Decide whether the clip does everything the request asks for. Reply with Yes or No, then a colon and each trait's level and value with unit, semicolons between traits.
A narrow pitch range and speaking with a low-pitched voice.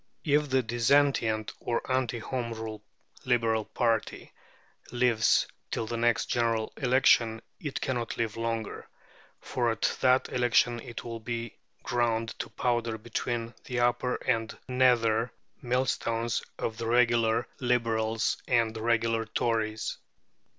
Yes: narrow, 1.5 semitones; low, 115 Hz